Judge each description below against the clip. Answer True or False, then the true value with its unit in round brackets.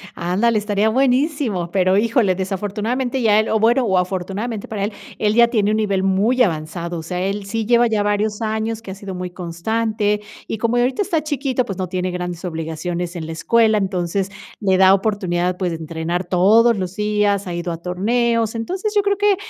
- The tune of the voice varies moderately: True (4.1 semitones)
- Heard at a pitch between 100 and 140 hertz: False (205 Hz)